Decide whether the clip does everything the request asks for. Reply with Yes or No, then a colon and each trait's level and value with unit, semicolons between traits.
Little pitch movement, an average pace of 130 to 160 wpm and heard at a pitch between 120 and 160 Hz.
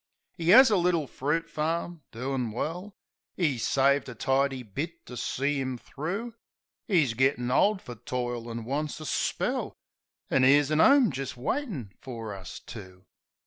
No: average, 5.3 semitones; average, 155 wpm; medium, 140 Hz